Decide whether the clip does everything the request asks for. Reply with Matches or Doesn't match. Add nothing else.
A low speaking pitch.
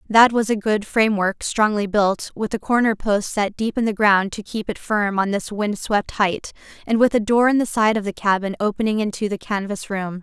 Doesn't match